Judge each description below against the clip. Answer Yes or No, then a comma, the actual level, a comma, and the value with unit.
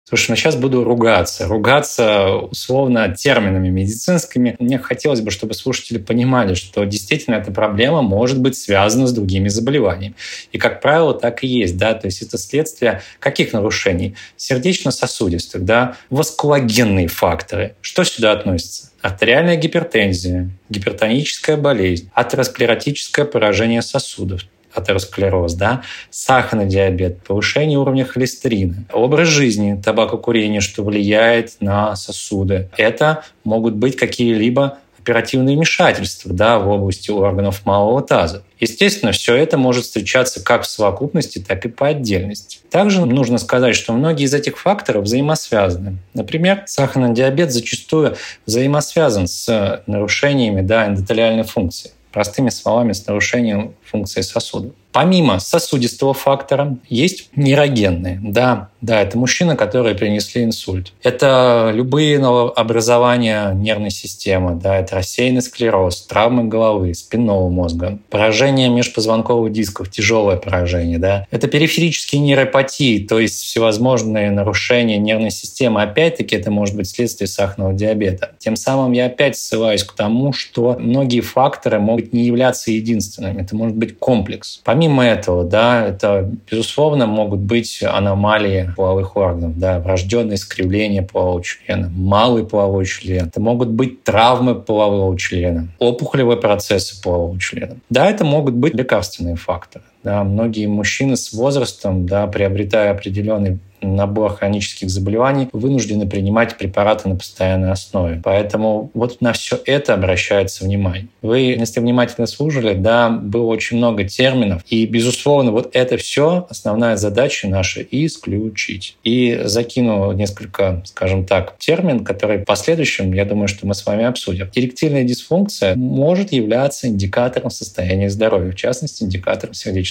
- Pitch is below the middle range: Yes, low, 110 Hz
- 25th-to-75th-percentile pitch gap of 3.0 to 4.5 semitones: Yes, average, 4.2 semitones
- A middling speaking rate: Yes, average, 130 wpm